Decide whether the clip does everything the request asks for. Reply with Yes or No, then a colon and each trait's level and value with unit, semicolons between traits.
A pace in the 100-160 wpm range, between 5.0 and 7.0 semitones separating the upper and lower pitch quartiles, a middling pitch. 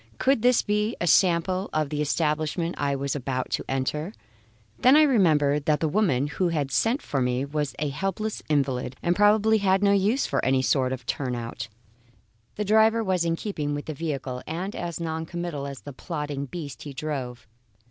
No: average, 185 wpm; wide, 5.6 semitones; medium, 155 Hz